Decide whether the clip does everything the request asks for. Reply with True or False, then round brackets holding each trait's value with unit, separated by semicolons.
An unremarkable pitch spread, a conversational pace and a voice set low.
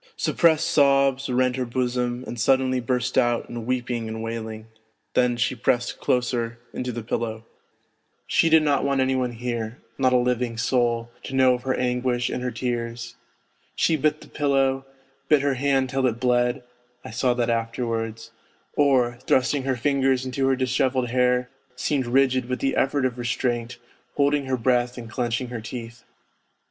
False (1.8 semitones; 170 wpm; 125 Hz)